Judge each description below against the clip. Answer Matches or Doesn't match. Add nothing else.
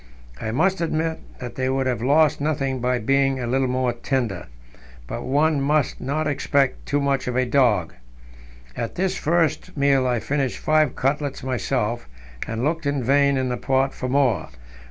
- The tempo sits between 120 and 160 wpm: Doesn't match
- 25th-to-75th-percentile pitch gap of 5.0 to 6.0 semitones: Doesn't match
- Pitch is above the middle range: Doesn't match